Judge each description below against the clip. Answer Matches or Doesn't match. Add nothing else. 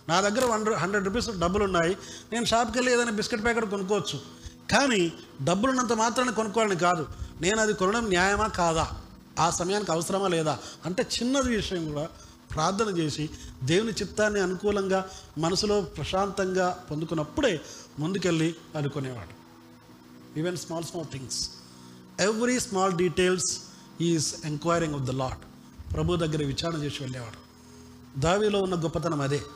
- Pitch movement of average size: Doesn't match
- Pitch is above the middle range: Doesn't match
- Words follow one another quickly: Matches